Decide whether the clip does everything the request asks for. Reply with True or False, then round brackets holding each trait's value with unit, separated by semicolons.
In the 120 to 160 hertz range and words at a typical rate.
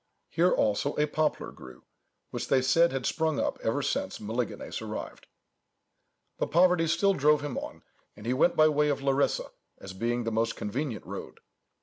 True (140 Hz; 175 wpm)